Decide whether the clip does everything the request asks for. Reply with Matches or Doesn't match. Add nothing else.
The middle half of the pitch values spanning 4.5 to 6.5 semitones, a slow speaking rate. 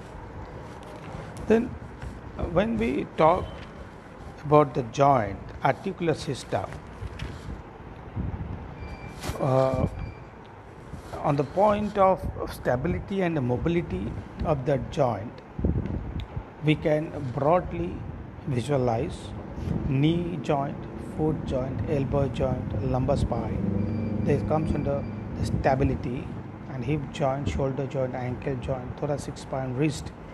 Matches